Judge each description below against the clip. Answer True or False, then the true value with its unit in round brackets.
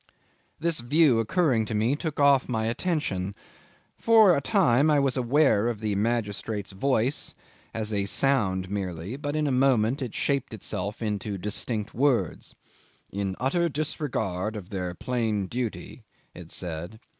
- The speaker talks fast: False (145 wpm)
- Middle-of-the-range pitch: False (115 Hz)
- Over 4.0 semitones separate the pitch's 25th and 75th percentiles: True (5.5 semitones)